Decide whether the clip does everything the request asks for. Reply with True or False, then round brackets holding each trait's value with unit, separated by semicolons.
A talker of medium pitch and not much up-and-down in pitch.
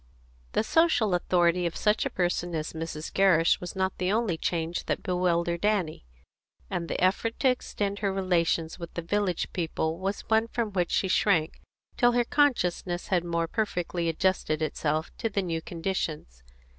False (180 Hz; 3.3 semitones)